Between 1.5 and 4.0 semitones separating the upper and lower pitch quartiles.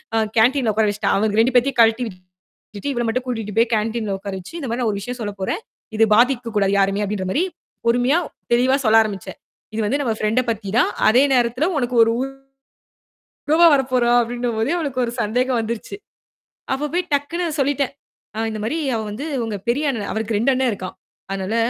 Yes: average, 3.3 semitones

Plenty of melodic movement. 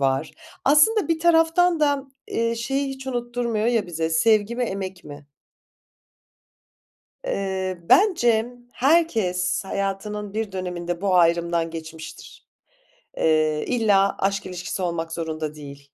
Yes: wide, 6.2 semitones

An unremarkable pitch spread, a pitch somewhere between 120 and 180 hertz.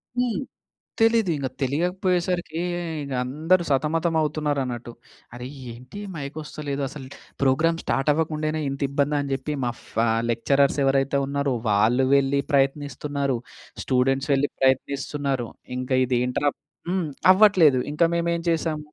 Yes: average, 3.2 semitones; medium, 140 Hz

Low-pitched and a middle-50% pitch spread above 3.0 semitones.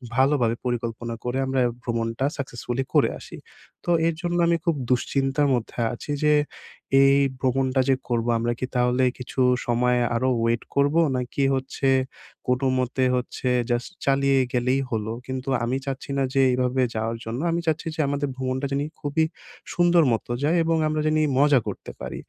No: low, 130 Hz; narrow, 2.5 semitones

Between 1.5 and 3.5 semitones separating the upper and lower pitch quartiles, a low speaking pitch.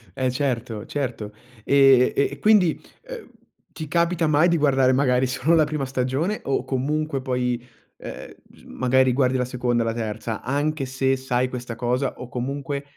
Yes: narrow, 2.5 semitones; low, 130 Hz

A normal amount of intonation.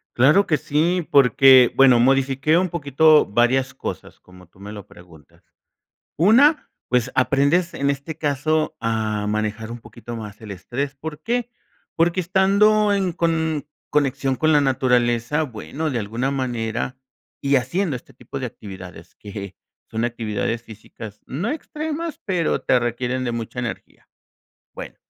No: wide, 5.7 semitones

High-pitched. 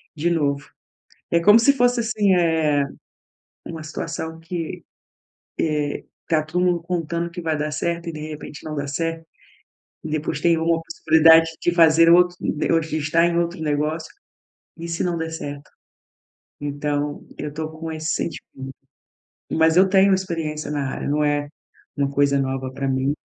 No: medium, 160 Hz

